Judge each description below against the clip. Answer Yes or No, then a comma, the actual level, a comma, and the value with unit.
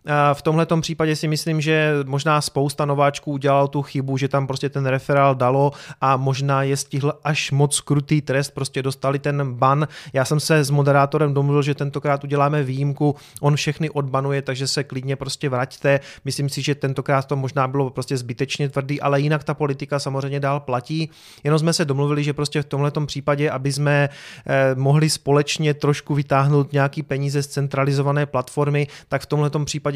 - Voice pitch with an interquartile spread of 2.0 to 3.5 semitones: No, narrow, 1.2 semitones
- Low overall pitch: No, medium, 145 Hz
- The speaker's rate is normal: No, fast, 180 wpm